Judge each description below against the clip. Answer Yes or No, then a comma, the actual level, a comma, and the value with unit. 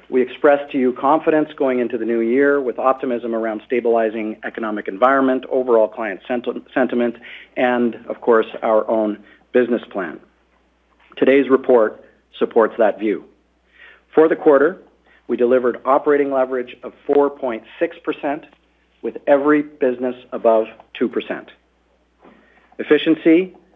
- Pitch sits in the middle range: No, low, 125 Hz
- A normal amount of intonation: Yes, average, 3.5 semitones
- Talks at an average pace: No, slow, 120 wpm